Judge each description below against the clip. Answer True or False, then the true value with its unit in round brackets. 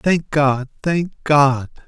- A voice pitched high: False (145 Hz)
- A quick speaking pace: False (130 wpm)